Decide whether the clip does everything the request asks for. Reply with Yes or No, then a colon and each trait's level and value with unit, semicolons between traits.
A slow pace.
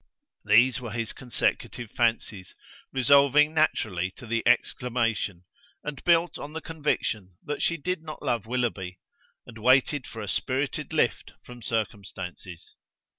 Yes: slow, 130 wpm